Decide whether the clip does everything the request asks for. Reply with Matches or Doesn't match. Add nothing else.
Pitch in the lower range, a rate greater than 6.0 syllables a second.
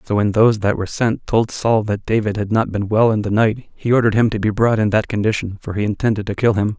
Matches